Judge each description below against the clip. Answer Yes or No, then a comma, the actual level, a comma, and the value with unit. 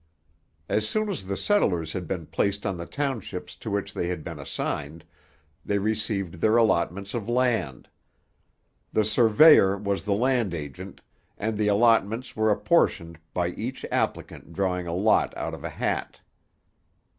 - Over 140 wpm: Yes, average, 155 wpm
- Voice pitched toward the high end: No, low, 100 Hz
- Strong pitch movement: No, average, 4.1 semitones